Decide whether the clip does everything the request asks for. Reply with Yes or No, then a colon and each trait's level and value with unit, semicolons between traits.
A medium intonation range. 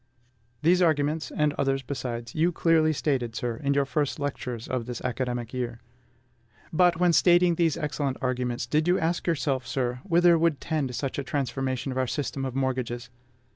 Yes: average, 4.1 semitones